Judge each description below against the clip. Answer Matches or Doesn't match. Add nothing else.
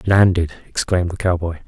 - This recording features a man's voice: Matches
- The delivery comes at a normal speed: Matches